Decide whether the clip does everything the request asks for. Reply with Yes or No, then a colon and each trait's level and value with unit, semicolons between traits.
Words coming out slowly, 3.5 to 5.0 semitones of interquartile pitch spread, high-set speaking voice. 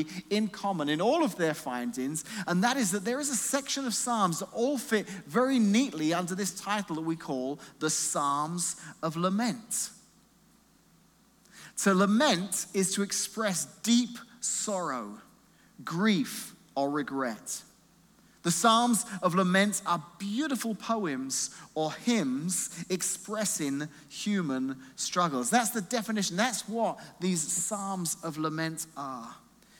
No: slow, 130 wpm; wide, 5.6 semitones; high, 195 Hz